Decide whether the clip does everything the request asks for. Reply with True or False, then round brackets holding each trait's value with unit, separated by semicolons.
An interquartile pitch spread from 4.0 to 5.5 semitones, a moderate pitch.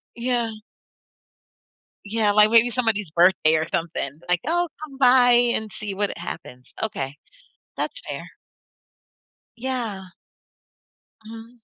False (4.4 semitones; 220 Hz)